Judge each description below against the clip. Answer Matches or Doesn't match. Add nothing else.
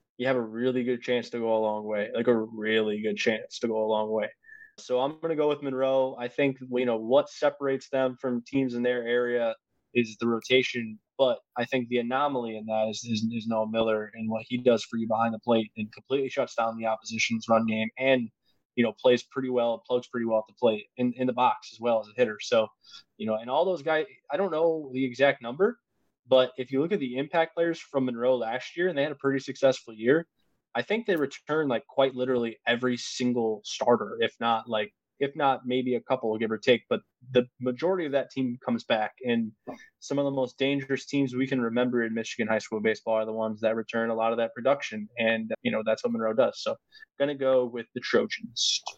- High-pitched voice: Doesn't match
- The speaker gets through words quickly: Matches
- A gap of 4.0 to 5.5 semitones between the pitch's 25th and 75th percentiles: Doesn't match